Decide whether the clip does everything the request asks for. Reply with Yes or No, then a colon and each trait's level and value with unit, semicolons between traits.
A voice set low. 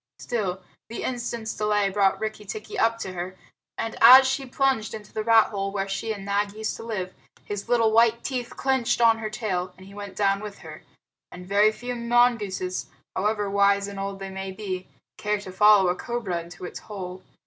No: high, 210 Hz